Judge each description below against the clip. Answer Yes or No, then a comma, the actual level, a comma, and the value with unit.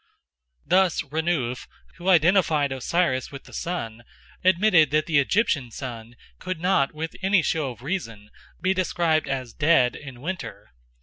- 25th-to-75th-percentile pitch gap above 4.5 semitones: Yes, wide, 5.6 semitones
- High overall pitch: No, medium, 155 Hz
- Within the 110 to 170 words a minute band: Yes, average, 140 wpm